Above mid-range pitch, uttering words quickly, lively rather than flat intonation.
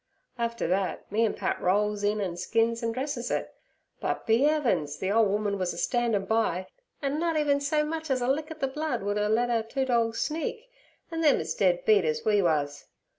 Yes: high, 225 Hz; fast, 220 wpm; wide, 5.7 semitones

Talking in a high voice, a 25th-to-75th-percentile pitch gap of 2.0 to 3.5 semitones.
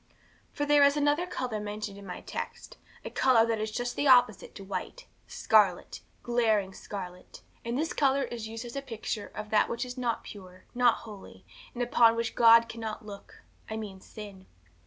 Yes: high, 230 Hz; average, 2.9 semitones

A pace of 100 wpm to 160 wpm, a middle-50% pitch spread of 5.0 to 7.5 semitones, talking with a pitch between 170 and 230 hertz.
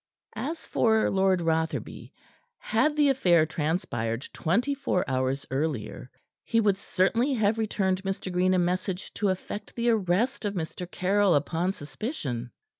Yes: average, 140 wpm; average, 5.3 semitones; medium, 185 Hz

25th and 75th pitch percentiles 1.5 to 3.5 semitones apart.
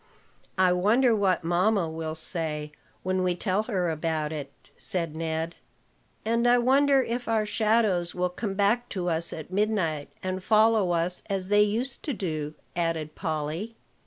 No: average, 4.8 semitones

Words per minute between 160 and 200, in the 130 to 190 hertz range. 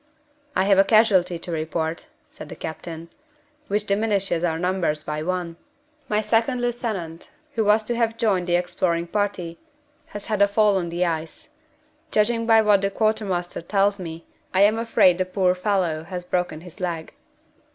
Yes: average, 170 wpm; medium, 185 Hz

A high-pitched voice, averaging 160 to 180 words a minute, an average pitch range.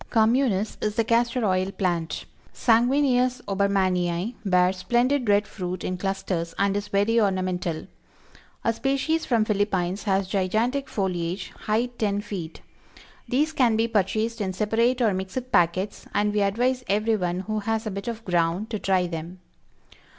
No: high, 205 Hz; average, 150 wpm; average, 3.7 semitones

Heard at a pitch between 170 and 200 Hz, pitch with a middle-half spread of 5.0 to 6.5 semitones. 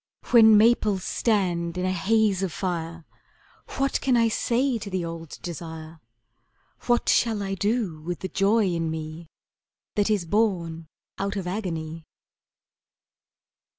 No: high, 190 Hz; average, 4.5 semitones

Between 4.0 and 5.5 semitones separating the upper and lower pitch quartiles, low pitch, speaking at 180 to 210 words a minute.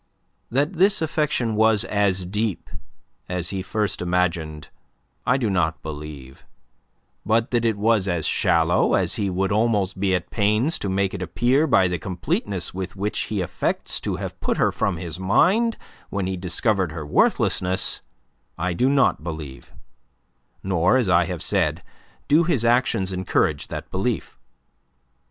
No: average, 4.4 semitones; very low, 95 Hz; average, 155 wpm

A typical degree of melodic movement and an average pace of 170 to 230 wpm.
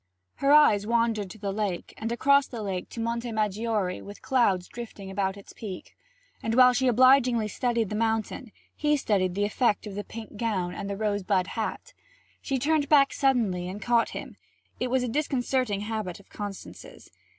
Yes: average, 3.7 semitones; average, 185 wpm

